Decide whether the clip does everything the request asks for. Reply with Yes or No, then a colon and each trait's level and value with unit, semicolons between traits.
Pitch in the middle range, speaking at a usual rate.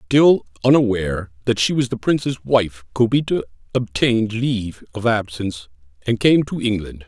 No: low, 110 Hz; average, 145 wpm